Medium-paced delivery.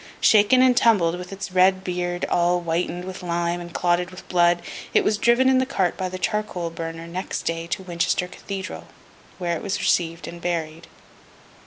Yes: average, 185 wpm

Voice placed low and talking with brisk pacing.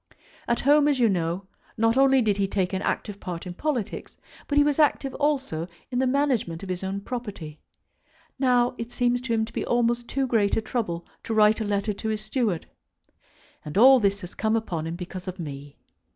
No: high, 220 Hz; fast, 210 wpm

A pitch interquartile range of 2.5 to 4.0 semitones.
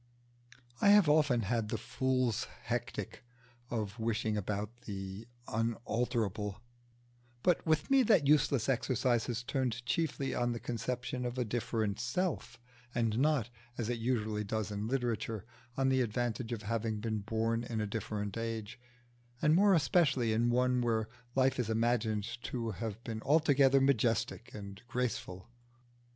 Yes: average, 2.8 semitones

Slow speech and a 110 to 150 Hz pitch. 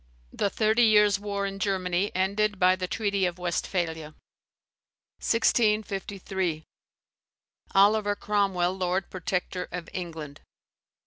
No: slow, 105 wpm; high, 190 Hz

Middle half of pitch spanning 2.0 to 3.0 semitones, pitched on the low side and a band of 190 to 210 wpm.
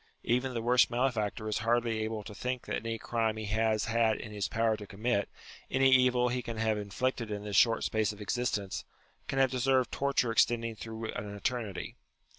Yes: narrow, 2.4 semitones; low, 115 Hz; average, 200 wpm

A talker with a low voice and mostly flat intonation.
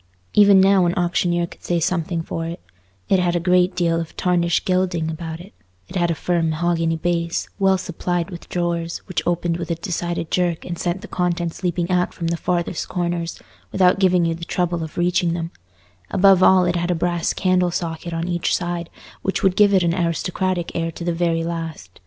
No: medium, 175 Hz; narrow, 1.2 semitones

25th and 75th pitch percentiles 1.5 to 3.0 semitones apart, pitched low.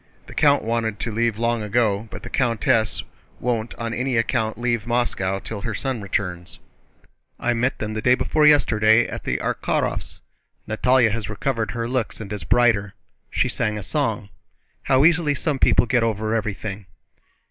Yes: narrow, 2.5 semitones; low, 115 Hz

